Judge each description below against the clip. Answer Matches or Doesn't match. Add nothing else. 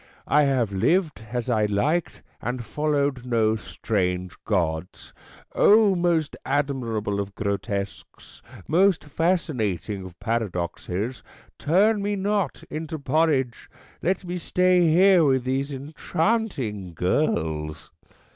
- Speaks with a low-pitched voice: Matches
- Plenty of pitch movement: Matches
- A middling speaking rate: Doesn't match